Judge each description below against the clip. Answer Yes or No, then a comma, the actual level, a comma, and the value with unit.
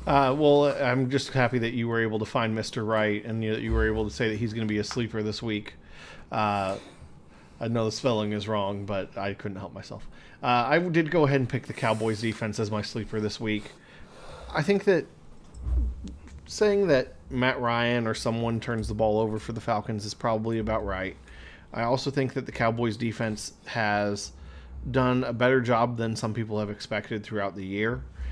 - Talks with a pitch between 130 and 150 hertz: No, low, 110 Hz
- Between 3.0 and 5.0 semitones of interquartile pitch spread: No, narrow, 2.5 semitones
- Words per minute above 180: Yes, fast, 205 wpm